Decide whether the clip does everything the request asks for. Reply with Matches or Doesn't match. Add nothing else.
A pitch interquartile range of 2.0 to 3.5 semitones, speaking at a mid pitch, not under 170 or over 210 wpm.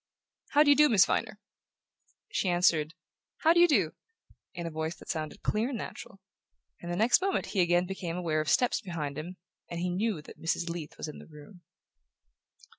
Doesn't match